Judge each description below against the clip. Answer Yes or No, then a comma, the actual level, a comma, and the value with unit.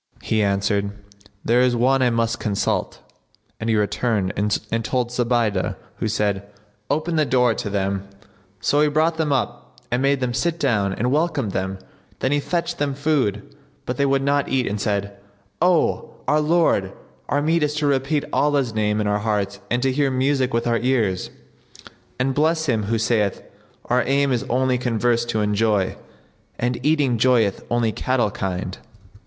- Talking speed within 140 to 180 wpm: Yes, average, 175 wpm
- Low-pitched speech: Yes, low, 120 Hz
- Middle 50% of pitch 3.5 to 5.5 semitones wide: Yes, average, 5.0 semitones